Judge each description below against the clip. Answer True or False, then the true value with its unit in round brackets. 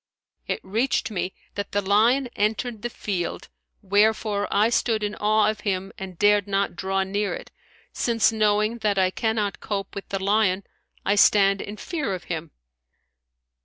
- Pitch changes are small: True (1.9 semitones)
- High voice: True (205 Hz)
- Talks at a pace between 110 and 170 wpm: True (165 wpm)